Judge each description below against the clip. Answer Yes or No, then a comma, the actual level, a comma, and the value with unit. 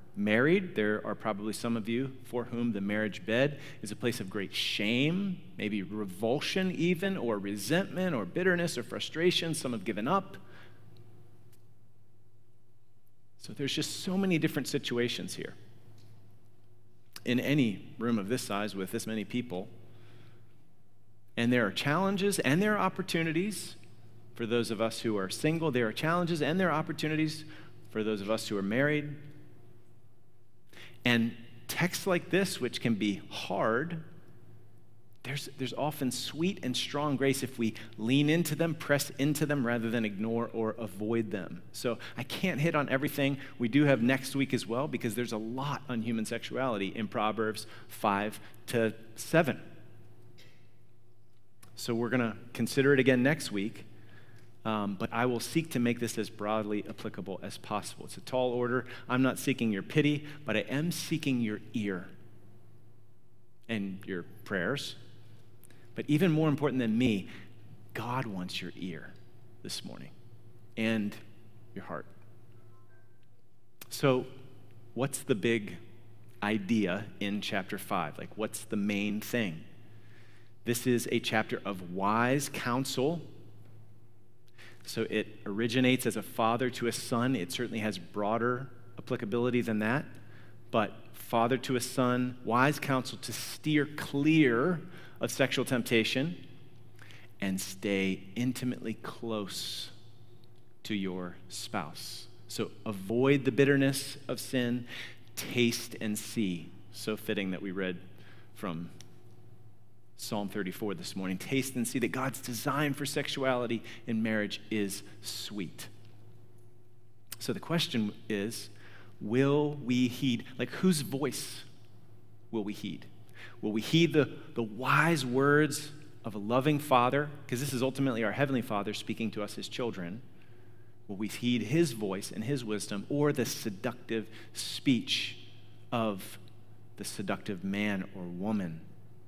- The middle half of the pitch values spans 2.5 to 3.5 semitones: Yes, average, 3.0 semitones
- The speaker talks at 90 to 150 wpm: Yes, average, 140 wpm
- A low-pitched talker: Yes, low, 115 Hz